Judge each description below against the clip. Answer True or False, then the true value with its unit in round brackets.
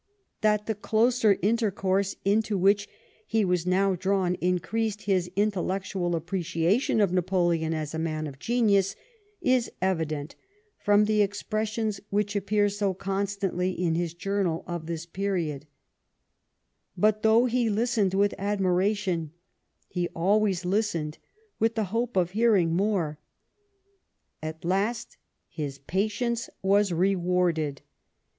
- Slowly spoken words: True (120 wpm)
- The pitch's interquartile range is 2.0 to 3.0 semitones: False (3.4 semitones)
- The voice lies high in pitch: True (195 Hz)